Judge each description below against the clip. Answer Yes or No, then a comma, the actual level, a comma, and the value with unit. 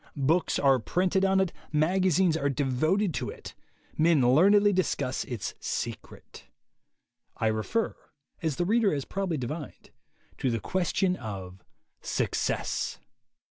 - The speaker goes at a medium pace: No, slow, 125 wpm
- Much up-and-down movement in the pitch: Yes, wide, 6.3 semitones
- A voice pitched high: No, medium, 160 Hz